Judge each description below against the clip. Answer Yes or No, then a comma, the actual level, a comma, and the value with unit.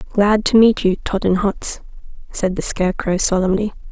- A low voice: No, high, 195 Hz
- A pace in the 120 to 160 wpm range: Yes, average, 140 wpm